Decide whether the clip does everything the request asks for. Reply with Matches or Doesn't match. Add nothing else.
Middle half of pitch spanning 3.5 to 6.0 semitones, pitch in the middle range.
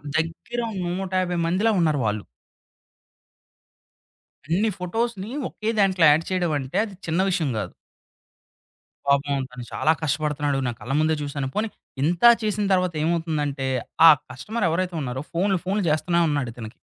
Matches